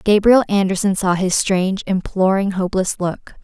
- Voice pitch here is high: Yes, high, 195 Hz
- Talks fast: No, average, 140 wpm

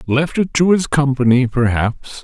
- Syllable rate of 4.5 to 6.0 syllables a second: No, 4.3 syllables/s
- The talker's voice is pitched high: No, low, 135 Hz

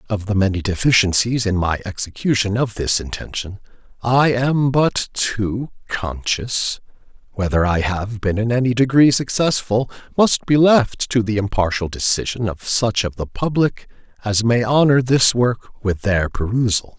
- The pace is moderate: Yes, average, 150 wpm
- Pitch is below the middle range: Yes, low, 115 Hz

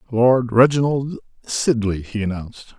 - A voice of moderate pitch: No, low, 120 Hz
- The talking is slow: Yes, slow, 110 wpm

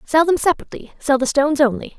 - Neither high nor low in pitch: No, very high, 285 Hz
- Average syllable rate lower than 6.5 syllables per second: No, 7.1 syllables/s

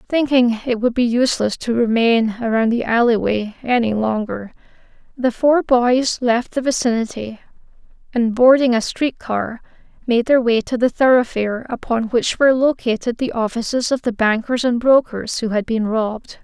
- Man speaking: No, female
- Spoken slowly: No, average, 160 wpm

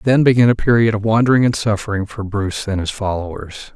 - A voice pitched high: No, low, 105 Hz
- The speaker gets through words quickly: Yes, fast, 210 wpm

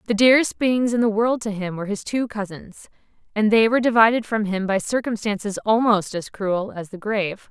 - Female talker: Yes, female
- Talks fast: Yes, fast, 210 wpm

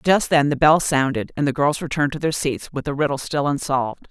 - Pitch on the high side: No, medium, 145 Hz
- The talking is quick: Yes, fast, 250 wpm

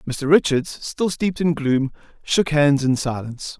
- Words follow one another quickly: No, average, 165 wpm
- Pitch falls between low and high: Yes, medium, 145 Hz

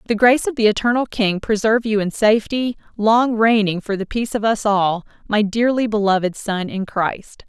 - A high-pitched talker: Yes, high, 215 Hz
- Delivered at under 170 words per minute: No, average, 195 wpm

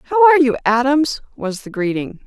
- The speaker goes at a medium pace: Yes, average, 185 wpm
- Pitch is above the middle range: Yes, very high, 260 Hz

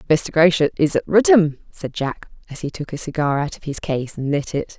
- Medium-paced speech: No, fast, 240 wpm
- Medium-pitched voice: Yes, medium, 160 Hz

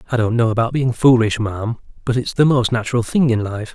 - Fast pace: Yes, fast, 240 wpm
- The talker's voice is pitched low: Yes, low, 120 Hz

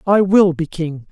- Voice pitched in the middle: Yes, medium, 175 Hz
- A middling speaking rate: No, fast, 215 wpm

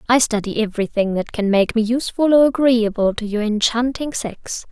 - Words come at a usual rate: Yes, average, 180 wpm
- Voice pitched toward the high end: Yes, high, 230 Hz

